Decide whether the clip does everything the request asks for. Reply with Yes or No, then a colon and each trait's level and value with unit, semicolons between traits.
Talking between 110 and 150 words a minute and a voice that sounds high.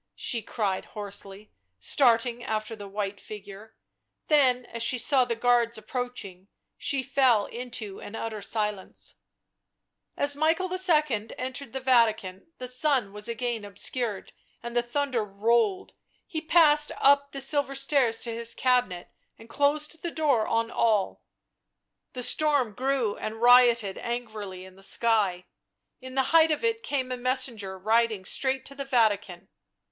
Yes: average, 145 wpm; high, 235 Hz